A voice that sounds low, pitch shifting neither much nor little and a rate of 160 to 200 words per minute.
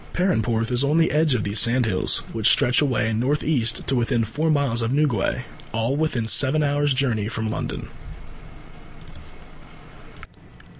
No: low, 125 Hz; average, 4.4 semitones; average, 145 wpm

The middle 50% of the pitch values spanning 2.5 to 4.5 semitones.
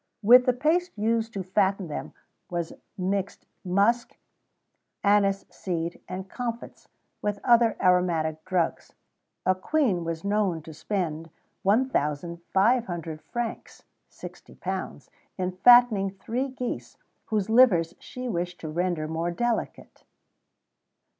No: average, 5.2 semitones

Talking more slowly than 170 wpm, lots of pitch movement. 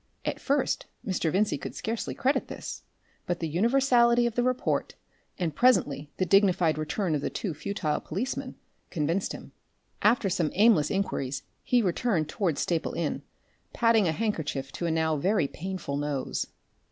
Yes: average, 150 wpm; wide, 6.5 semitones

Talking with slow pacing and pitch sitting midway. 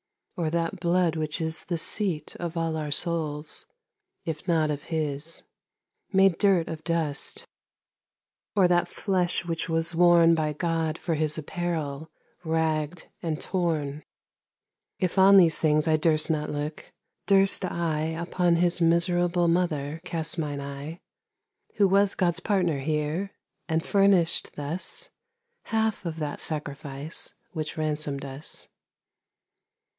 Yes: slow, 115 wpm; medium, 165 Hz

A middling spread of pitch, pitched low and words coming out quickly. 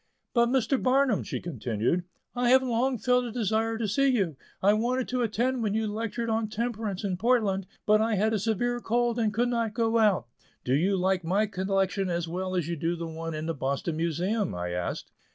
No: average, 4.7 semitones; high, 215 Hz; fast, 210 wpm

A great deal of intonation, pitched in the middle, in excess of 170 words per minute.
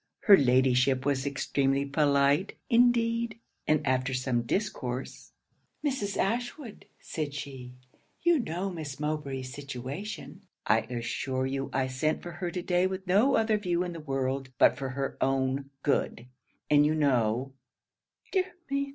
No: wide, 6.3 semitones; medium, 145 Hz; average, 145 wpm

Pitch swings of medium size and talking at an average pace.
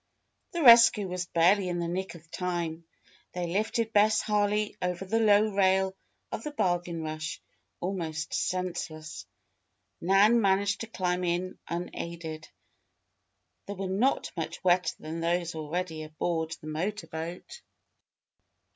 No: average, 3.3 semitones; slow, 130 wpm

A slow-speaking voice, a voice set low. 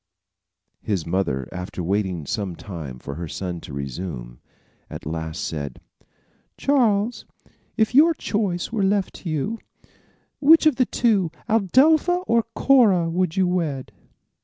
No: slow, 130 wpm; medium, 165 Hz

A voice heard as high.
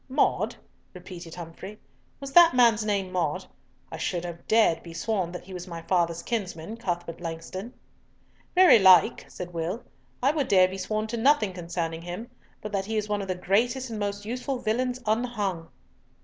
Yes: high, 195 Hz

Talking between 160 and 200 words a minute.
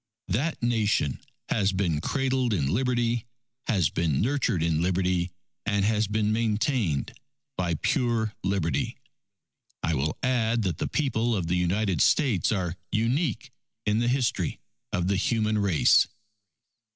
No: slow, 135 wpm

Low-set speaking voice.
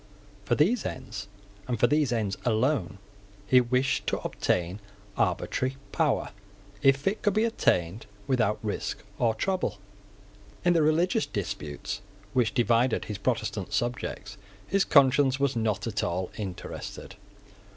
Yes: low, 120 Hz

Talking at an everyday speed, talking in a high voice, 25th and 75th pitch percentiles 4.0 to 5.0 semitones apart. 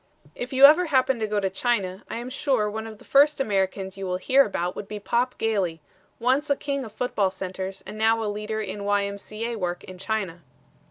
No: fast, 230 wpm; high, 215 Hz; average, 4.3 semitones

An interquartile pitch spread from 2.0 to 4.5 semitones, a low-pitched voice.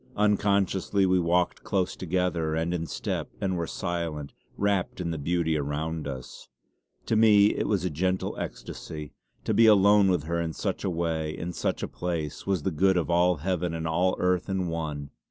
Yes: average, 2.8 semitones; very low, 90 Hz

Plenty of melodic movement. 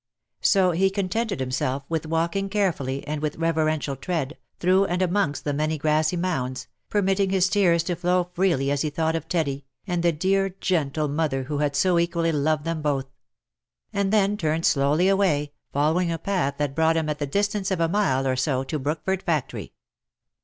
No: average, 4.1 semitones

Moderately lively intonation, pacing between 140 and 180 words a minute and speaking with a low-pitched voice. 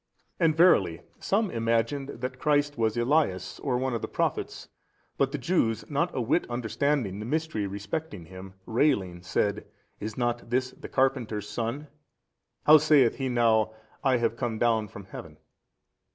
Yes: average, 4.8 semitones; average, 160 wpm; low, 120 Hz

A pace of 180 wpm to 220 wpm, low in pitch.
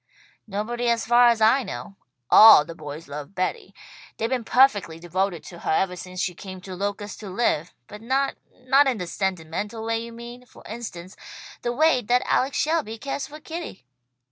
No: average, 185 wpm; high, 215 Hz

